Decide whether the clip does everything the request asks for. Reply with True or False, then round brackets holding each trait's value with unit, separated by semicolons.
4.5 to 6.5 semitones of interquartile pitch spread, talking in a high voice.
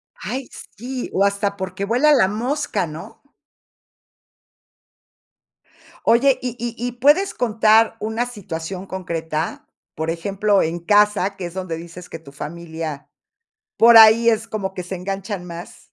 True (4.9 semitones; 200 Hz)